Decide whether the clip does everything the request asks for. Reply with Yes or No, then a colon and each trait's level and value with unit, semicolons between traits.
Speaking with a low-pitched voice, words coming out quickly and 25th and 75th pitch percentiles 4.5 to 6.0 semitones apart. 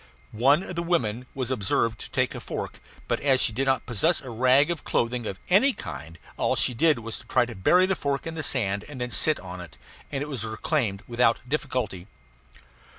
Yes: low, 125 Hz; fast, 220 wpm; average, 5.2 semitones